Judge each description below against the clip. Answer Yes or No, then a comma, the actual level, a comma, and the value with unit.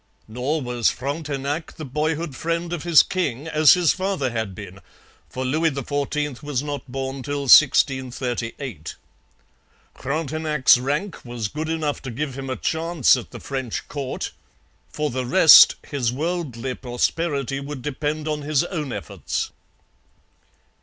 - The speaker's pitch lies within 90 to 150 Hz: Yes, medium, 140 Hz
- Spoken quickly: No, average, 140 wpm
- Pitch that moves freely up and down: No, average, 3.3 semitones